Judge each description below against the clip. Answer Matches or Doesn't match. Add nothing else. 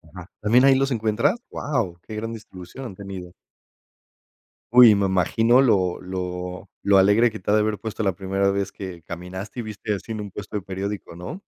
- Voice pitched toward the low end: Matches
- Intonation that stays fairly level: Doesn't match